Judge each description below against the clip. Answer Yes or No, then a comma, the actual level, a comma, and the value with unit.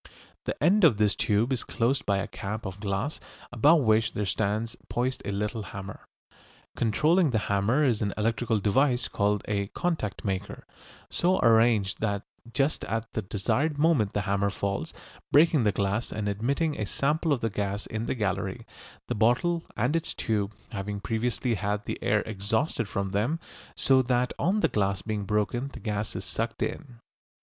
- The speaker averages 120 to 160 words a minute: No, average, 175 wpm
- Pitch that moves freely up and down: No, average, 4.2 semitones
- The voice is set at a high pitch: No, low, 110 Hz